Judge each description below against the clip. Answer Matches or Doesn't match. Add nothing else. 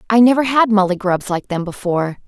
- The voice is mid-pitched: Doesn't match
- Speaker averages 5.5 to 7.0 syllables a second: Matches